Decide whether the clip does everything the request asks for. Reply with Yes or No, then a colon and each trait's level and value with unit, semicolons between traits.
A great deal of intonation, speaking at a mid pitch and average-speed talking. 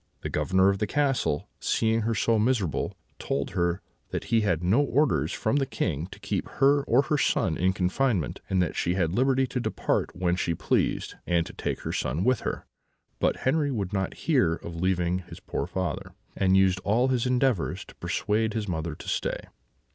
No: wide, 6.0 semitones; very low, 95 Hz; average, 195 wpm